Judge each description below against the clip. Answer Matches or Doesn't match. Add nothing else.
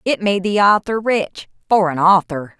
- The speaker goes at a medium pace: Matches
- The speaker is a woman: Matches